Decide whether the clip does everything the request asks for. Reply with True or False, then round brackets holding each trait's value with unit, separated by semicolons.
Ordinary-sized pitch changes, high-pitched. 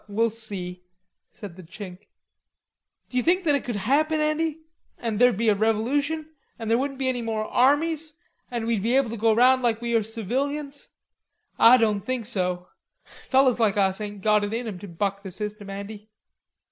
True (4.2 semitones; 225 Hz)